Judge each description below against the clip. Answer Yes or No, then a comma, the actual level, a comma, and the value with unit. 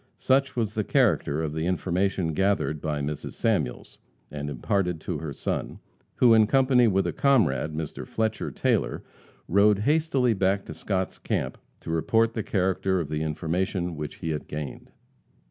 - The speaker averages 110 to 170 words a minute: Yes, average, 165 wpm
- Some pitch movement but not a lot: No, wide, 5.9 semitones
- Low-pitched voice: Yes, very low, 95 Hz